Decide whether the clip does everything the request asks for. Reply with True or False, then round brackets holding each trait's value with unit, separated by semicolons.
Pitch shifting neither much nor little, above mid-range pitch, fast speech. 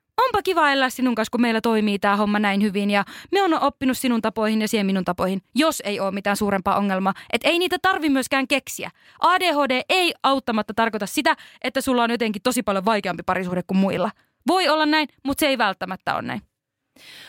False (6.0 semitones; 235 Hz; 200 wpm)